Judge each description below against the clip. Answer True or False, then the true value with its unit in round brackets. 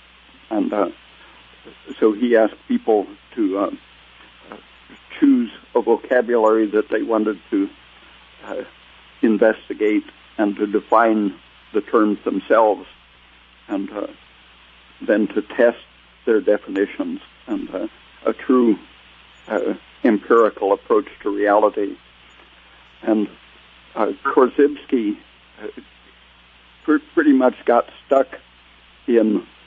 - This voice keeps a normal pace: False (95 wpm)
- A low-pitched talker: True (110 Hz)